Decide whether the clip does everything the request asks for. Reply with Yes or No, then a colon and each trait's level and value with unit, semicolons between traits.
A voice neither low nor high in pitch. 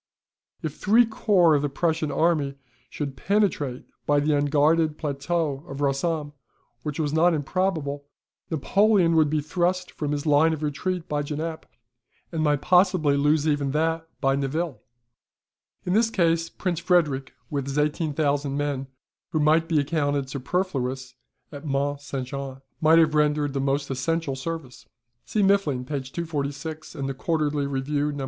Yes: medium, 150 Hz